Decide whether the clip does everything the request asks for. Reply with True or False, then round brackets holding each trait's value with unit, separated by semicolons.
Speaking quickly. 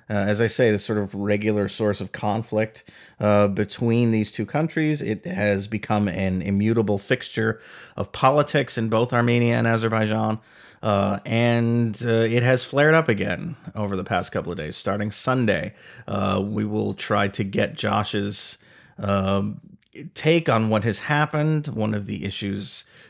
False (160 wpm)